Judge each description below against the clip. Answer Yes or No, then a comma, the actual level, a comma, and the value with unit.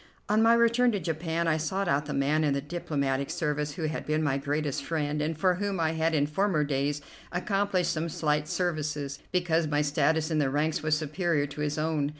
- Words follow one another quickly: Yes, fast, 210 wpm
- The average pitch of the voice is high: No, medium, 155 Hz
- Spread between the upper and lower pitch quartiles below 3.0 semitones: Yes, narrow, 2.6 semitones